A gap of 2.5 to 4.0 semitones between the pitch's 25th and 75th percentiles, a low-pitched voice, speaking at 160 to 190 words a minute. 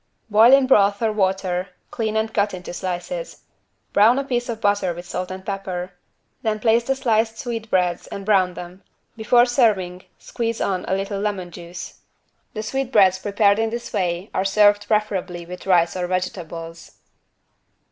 No: average, 3.5 semitones; high, 200 Hz; average, 165 wpm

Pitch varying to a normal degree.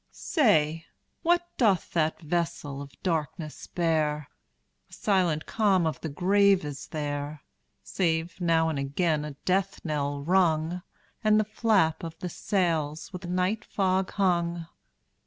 Yes: average, 3.7 semitones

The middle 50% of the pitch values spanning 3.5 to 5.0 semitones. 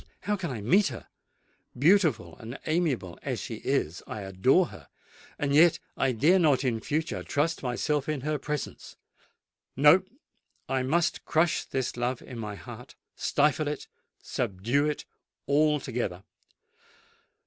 Yes: average, 4.5 semitones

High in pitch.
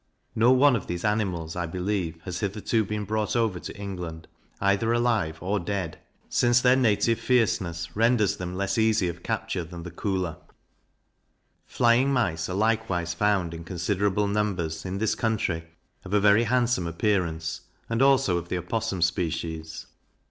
No: low, 100 Hz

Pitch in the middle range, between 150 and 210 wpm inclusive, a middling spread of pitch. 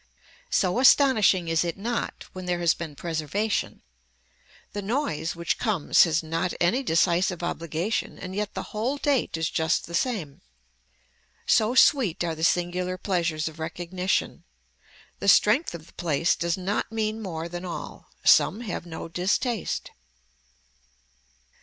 No: medium, 180 Hz; average, 140 wpm; average, 4.3 semitones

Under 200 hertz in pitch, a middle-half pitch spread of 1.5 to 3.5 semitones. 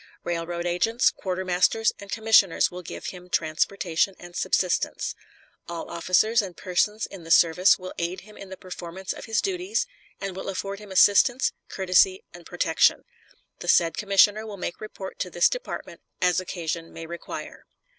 Yes: medium, 185 Hz; average, 3.1 semitones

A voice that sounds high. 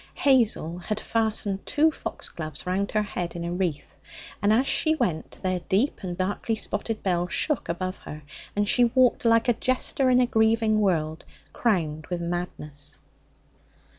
Yes: high, 200 Hz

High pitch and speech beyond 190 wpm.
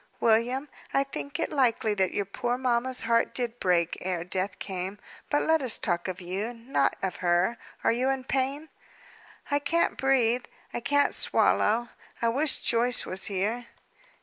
No: high, 235 Hz; average, 165 wpm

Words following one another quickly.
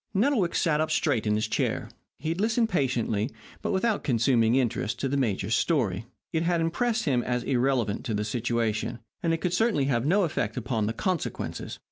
No: average, 190 wpm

